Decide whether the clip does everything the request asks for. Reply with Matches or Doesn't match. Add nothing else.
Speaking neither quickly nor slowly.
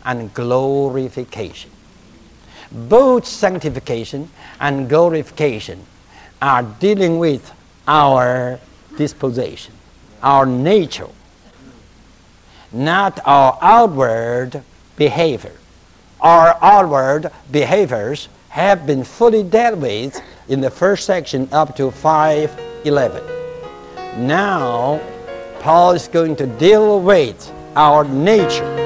Doesn't match